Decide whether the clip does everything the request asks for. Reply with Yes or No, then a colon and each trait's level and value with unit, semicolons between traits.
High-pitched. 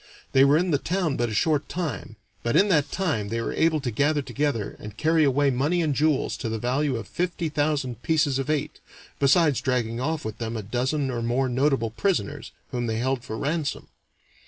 No: medium, 140 Hz